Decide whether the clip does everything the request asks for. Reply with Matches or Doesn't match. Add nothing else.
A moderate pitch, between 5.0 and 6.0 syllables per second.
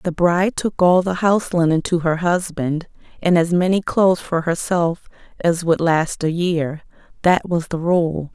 Doesn't match